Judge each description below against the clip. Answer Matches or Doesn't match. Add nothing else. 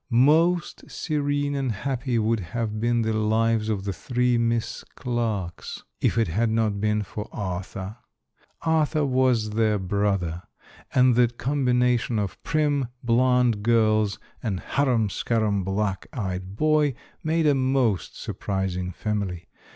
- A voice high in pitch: Doesn't match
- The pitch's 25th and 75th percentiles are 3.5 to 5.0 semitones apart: Matches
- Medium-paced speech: Doesn't match